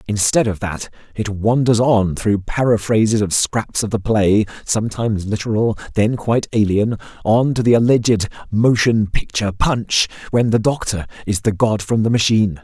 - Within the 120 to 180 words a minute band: Yes, average, 160 wpm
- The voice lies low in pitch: Yes, low, 110 Hz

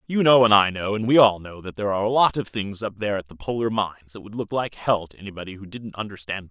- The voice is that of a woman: No, male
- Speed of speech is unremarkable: No, fast, 315 wpm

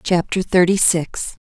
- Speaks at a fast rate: No, slow, 125 wpm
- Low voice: No, medium, 180 Hz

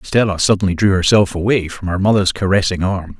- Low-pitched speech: Yes, very low, 95 Hz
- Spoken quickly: No, average, 190 wpm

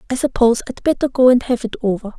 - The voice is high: Yes, high, 245 Hz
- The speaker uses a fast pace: Yes, fast, 245 wpm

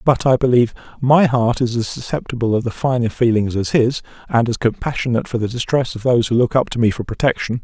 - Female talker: No, male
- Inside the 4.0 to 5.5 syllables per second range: No, 6.3 syllables/s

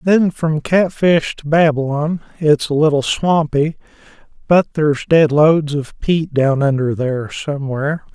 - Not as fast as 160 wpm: Yes, average, 140 wpm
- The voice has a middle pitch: Yes, medium, 150 Hz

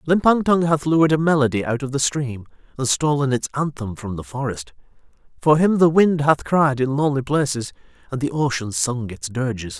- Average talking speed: Yes, average, 195 wpm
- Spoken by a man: Yes, male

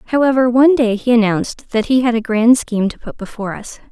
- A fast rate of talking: Yes, fast, 230 wpm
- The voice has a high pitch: Yes, high, 235 Hz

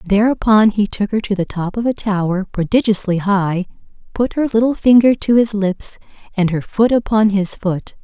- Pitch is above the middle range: Yes, high, 205 Hz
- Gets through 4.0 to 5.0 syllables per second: Yes, 4.9 syllables/s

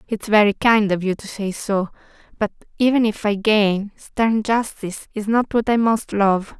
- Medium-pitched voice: No, high, 210 Hz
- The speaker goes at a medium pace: Yes, average, 190 wpm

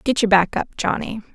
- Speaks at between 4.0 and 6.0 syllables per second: Yes, 5.7 syllables/s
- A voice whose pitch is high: Yes, high, 215 Hz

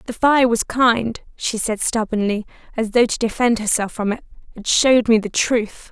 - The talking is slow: No, average, 195 wpm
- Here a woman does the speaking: Yes, female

